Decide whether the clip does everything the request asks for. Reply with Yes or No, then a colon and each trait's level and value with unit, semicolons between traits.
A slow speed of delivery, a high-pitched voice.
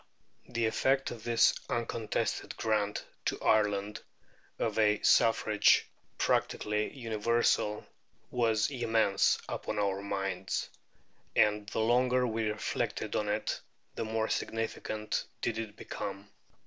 No: slow, 110 wpm; low, 110 Hz